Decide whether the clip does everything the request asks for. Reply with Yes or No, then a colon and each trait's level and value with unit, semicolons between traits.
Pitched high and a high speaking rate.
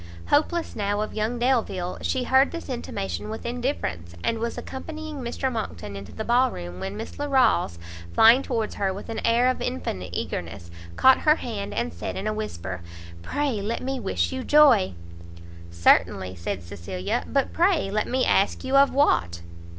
No: high, 220 Hz; average, 170 wpm